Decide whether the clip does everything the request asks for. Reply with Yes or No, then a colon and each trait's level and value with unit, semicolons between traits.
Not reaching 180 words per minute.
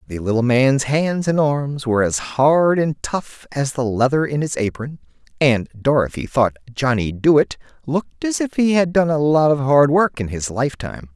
No: average, 195 wpm